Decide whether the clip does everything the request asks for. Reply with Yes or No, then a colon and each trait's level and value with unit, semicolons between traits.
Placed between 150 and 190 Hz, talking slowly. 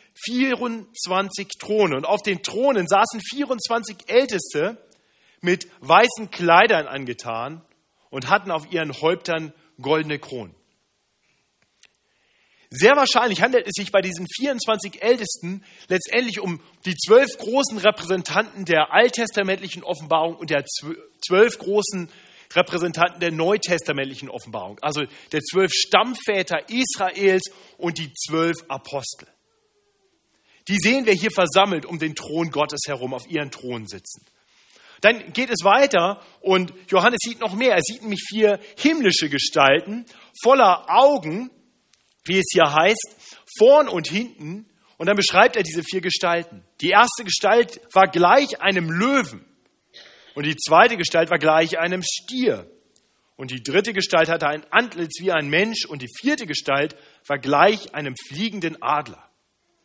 No: medium, 185 Hz; average, 135 wpm